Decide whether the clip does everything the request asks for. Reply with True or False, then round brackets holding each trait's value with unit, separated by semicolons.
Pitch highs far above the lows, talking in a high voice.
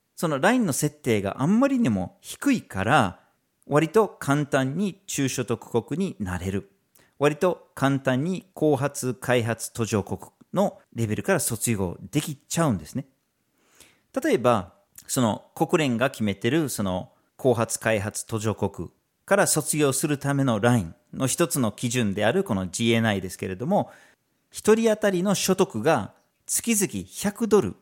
False (6.9 semitones; 130 Hz)